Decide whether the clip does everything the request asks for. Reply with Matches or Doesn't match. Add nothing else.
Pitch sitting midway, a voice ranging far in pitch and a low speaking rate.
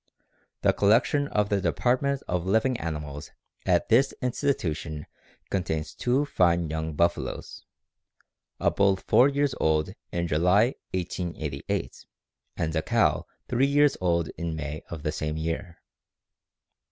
Doesn't match